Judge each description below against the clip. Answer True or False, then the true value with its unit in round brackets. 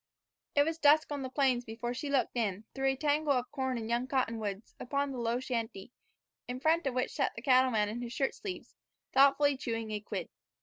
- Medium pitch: False (255 Hz)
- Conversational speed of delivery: False (210 wpm)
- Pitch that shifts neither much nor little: True (3.2 semitones)